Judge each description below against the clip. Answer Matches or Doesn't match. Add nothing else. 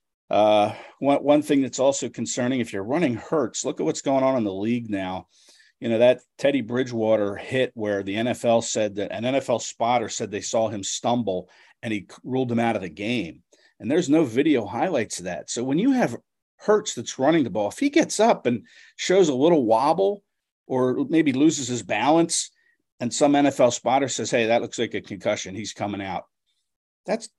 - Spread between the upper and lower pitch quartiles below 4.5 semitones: Doesn't match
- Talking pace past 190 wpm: Matches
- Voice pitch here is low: Matches